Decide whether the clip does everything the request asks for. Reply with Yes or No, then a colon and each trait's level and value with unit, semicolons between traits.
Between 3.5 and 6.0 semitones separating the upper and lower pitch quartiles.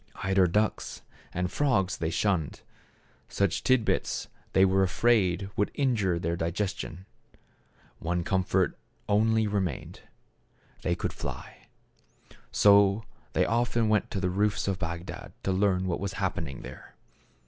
No: narrow, 2.6 semitones